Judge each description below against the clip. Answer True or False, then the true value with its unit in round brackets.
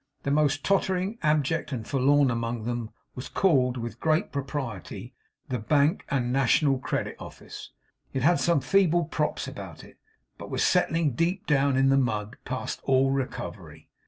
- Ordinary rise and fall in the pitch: True (3.6 semitones)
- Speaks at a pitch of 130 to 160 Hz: True (135 Hz)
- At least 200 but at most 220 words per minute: False (160 wpm)